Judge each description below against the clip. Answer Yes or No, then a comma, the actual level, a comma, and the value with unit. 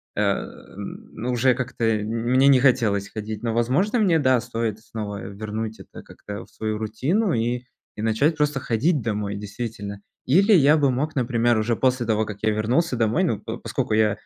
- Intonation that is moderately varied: Yes, average, 3.6 semitones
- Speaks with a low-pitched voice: Yes, low, 115 Hz